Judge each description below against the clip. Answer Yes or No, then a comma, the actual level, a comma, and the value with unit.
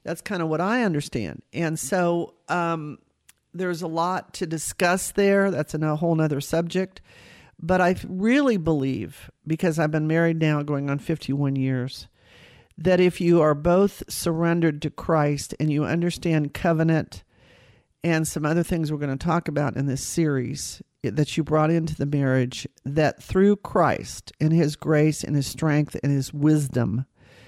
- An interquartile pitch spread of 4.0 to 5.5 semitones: No, average, 2.9 semitones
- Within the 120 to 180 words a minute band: Yes, average, 165 wpm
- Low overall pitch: No, medium, 160 Hz